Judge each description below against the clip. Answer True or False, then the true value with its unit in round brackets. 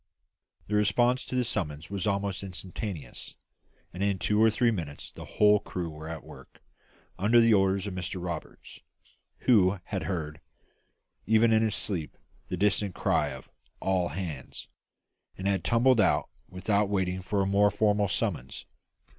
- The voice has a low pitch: True (100 Hz)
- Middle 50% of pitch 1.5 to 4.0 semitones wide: True (2.9 semitones)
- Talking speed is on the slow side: False (155 wpm)